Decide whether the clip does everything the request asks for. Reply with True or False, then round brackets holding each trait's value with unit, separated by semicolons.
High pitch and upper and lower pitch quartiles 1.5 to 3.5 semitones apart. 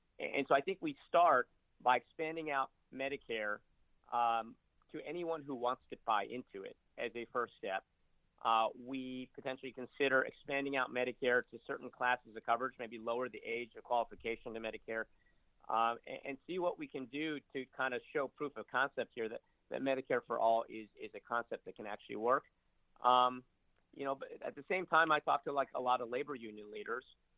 False (125 Hz; 3.1 semitones)